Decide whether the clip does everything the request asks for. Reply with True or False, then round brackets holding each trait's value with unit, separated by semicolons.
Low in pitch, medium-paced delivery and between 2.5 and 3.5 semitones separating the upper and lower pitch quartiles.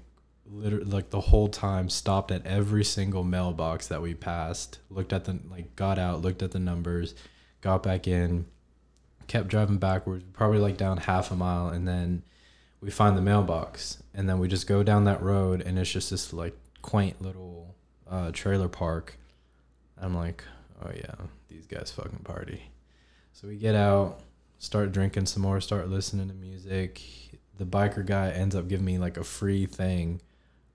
True (90 Hz; 175 wpm; 2.8 semitones)